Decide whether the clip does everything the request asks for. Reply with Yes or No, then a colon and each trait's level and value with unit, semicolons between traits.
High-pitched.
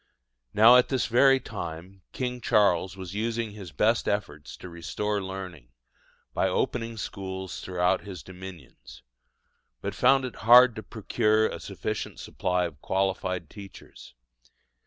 No: very low, 95 Hz